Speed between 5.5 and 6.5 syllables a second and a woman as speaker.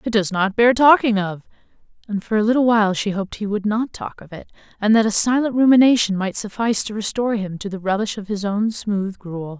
Yes: 5.8 syllables/s; female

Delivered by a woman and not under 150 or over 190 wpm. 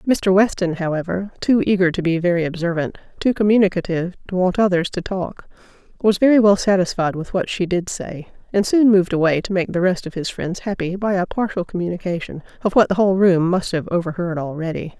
No: female; average, 200 wpm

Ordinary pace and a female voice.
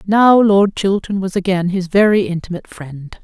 Yes: average, 165 wpm; female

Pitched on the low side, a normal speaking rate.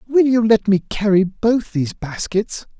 No: high, 205 Hz; average, 170 wpm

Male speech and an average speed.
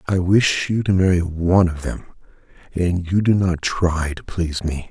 Yes: male; average, 195 wpm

